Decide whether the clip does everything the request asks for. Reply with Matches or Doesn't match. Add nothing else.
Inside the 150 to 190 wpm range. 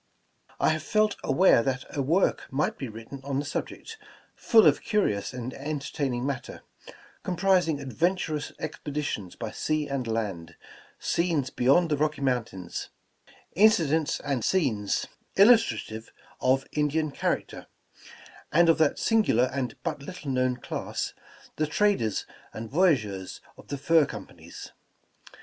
Doesn't match